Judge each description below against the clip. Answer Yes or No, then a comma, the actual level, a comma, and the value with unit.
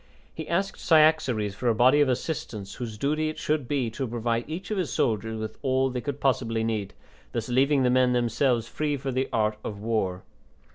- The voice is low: Yes, low, 125 Hz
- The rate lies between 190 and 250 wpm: Yes, average, 200 wpm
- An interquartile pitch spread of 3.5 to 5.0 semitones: Yes, average, 4.4 semitones